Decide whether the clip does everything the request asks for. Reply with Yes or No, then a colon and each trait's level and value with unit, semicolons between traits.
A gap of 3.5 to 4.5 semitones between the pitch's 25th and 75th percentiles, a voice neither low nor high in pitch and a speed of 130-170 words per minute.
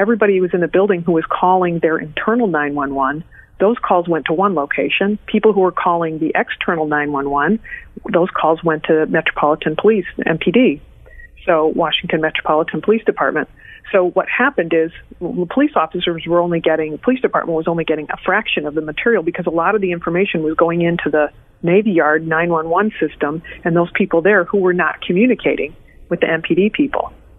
No: average, 3.8 semitones; medium, 175 Hz; fast, 205 wpm